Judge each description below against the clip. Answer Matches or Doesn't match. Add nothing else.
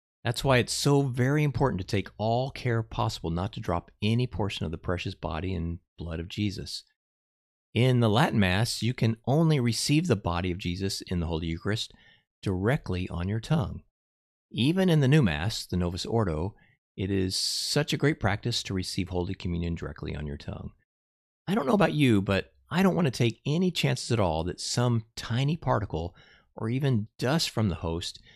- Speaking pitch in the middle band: Doesn't match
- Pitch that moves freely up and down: Matches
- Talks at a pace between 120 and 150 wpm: Doesn't match